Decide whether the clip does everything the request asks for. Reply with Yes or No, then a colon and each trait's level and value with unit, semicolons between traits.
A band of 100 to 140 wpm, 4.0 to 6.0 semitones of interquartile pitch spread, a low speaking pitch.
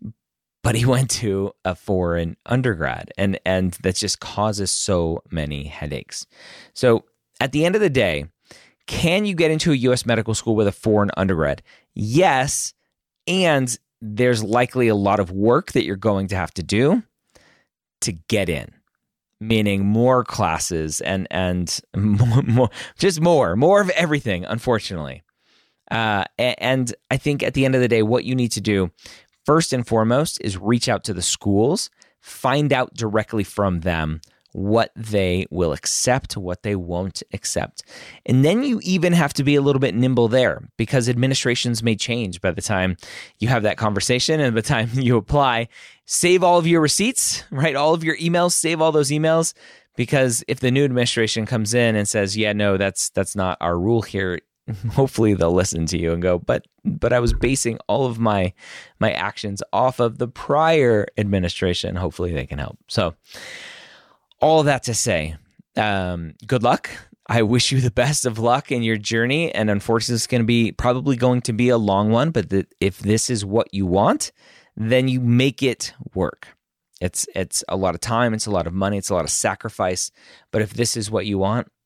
No: average, 185 wpm; average, 4.7 semitones; low, 115 Hz